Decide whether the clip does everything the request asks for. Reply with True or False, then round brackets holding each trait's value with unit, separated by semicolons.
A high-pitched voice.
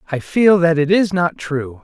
False (160 Hz)